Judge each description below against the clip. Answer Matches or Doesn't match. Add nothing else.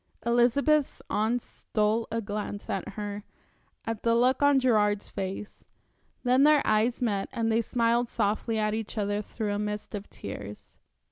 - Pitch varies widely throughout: Doesn't match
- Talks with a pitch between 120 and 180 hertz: Doesn't match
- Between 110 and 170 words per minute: Matches